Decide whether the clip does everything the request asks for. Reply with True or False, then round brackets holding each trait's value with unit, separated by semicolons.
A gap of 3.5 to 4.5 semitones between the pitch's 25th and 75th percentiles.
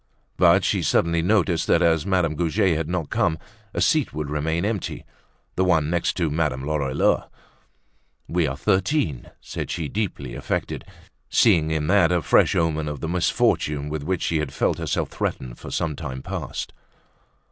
False (3.0 semitones)